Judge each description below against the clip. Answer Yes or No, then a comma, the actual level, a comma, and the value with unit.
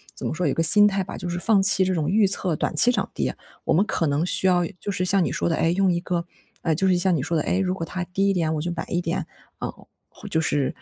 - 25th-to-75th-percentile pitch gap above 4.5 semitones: No, average, 2.7 semitones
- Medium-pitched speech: Yes, medium, 180 Hz